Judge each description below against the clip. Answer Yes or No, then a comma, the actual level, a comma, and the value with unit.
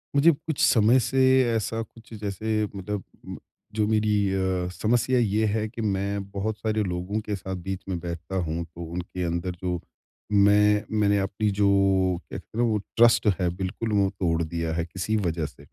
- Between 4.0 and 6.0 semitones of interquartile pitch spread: No, average, 3.2 semitones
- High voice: No, low, 100 Hz